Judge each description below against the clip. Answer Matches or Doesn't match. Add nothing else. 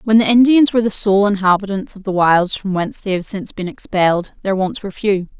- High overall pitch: Matches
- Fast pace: Matches